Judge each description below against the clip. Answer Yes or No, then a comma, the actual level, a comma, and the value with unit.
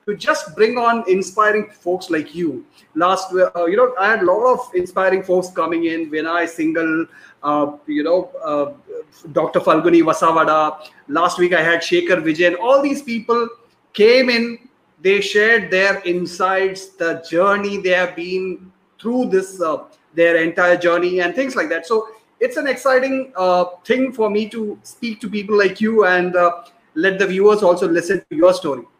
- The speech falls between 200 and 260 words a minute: No, average, 180 wpm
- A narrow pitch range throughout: No, average, 4.4 semitones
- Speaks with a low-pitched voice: No, medium, 185 Hz